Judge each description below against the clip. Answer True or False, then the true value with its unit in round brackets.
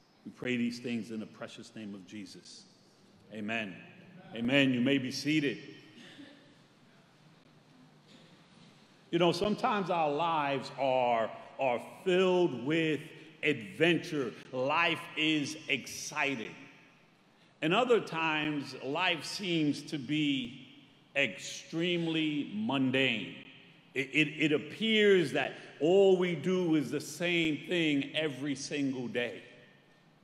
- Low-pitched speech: False (150 Hz)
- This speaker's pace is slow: True (105 wpm)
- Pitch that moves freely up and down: False (4.1 semitones)